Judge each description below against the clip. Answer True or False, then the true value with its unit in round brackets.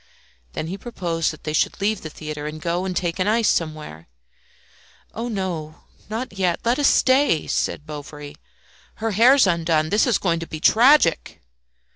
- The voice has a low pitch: False (175 Hz)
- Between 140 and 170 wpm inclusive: True (165 wpm)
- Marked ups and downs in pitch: True (5.7 semitones)